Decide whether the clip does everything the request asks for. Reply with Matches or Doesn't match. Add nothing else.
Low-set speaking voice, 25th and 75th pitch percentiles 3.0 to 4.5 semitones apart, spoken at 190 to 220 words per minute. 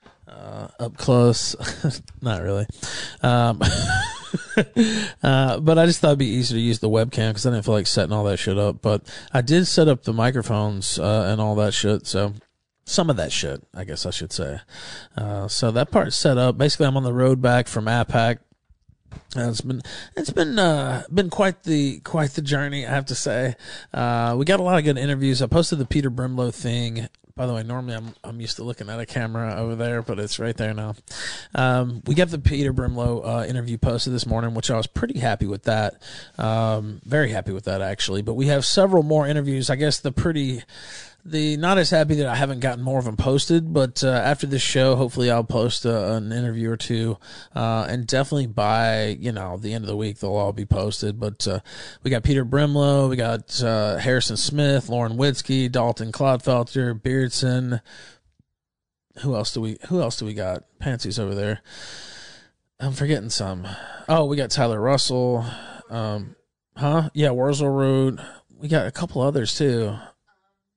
Matches